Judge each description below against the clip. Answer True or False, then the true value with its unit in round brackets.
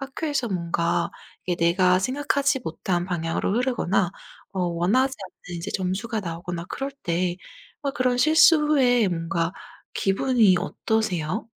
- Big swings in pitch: True (6.6 semitones)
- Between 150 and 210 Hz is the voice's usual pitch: True (190 Hz)